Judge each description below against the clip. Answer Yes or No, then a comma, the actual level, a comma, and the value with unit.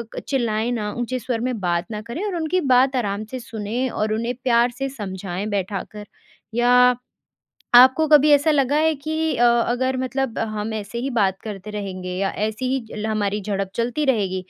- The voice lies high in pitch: Yes, high, 235 Hz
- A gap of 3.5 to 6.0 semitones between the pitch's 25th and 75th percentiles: Yes, average, 3.9 semitones